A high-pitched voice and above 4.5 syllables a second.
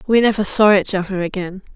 Yes: high, 195 Hz; 5.9 syllables/s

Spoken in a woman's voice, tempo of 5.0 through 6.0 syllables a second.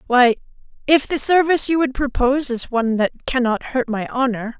Yes: female; 5.4 syllables/s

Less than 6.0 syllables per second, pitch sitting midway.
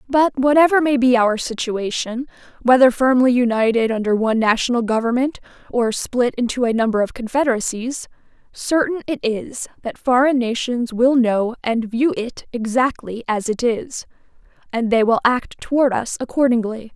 No: 4.9 syllables/s; high, 245 Hz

